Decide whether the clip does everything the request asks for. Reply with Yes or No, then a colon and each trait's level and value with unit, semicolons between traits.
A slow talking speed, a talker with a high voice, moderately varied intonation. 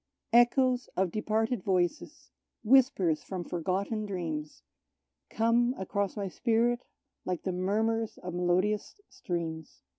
Yes: slow, 110 wpm; high, 200 Hz; average, 4.2 semitones